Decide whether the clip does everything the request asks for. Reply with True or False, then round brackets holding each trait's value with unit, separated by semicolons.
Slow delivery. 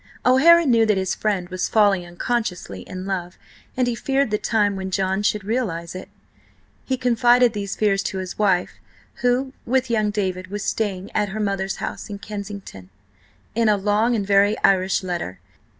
False (175 wpm)